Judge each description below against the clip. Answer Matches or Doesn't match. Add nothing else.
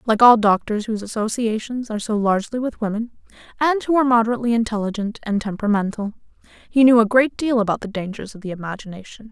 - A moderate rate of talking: Matches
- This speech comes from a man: Doesn't match